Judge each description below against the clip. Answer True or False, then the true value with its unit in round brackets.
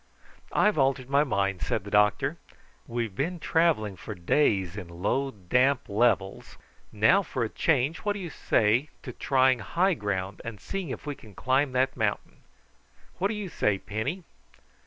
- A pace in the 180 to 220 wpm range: False (165 wpm)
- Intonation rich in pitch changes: True (6.3 semitones)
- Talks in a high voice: False (125 Hz)